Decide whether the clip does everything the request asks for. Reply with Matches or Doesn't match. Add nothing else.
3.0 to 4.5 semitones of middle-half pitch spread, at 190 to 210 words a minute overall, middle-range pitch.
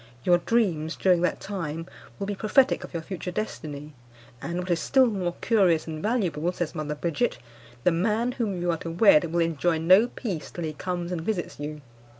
Matches